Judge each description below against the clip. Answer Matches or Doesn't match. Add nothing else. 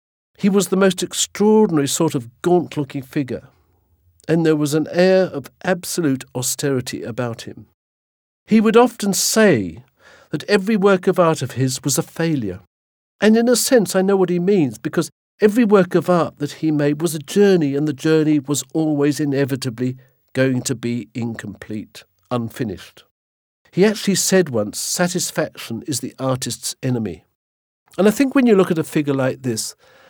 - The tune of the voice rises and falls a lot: Matches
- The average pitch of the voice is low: Doesn't match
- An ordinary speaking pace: Matches